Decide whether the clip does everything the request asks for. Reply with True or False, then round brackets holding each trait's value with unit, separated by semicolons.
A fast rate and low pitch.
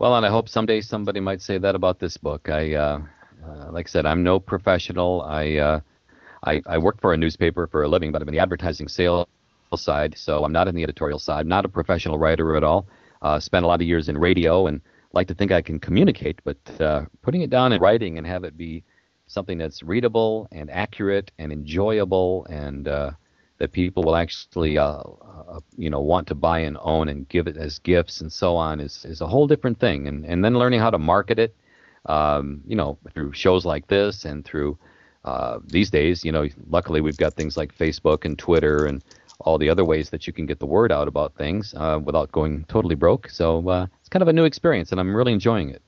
True (230 wpm; 85 Hz)